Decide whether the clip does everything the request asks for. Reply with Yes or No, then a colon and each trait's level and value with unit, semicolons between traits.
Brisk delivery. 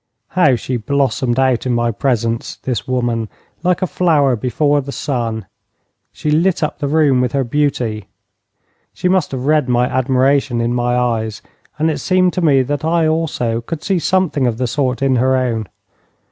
No: average, 180 wpm